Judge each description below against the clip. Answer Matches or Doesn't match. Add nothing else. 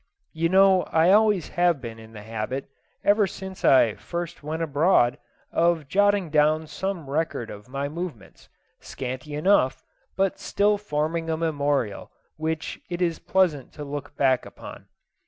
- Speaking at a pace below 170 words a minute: Matches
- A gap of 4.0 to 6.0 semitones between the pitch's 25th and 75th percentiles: Matches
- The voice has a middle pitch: Matches